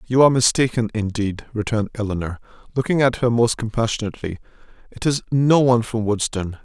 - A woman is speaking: No, male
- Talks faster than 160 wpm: No, average, 155 wpm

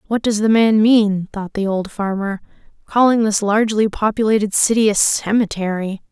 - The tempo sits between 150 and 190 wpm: Yes, average, 155 wpm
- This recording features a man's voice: No, female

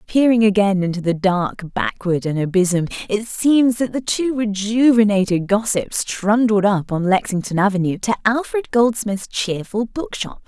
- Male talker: No, female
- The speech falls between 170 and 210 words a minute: No, average, 145 wpm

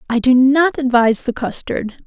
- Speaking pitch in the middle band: No, very high, 255 Hz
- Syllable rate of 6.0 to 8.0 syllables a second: No, 5.0 syllables/s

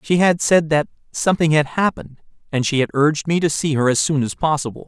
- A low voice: No, medium, 155 Hz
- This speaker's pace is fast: Yes, fast, 235 wpm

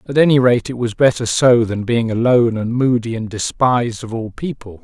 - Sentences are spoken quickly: Yes, fast, 210 wpm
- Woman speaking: No, male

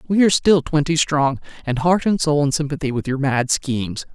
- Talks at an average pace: No, fast, 215 wpm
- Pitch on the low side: No, medium, 150 Hz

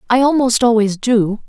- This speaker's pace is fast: No, average, 160 wpm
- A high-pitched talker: Yes, high, 235 Hz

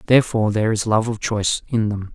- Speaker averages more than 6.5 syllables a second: Yes, 6.7 syllables/s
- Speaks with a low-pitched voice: Yes, low, 110 Hz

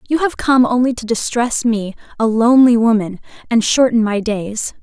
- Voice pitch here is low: No, high, 230 Hz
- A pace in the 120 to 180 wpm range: Yes, average, 175 wpm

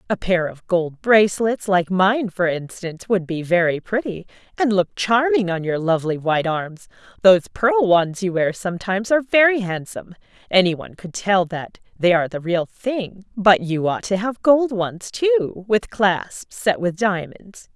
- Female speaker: Yes, female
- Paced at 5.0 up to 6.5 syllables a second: No, 4.6 syllables/s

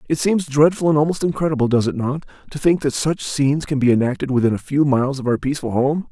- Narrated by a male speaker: Yes, male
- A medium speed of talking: No, fast, 225 wpm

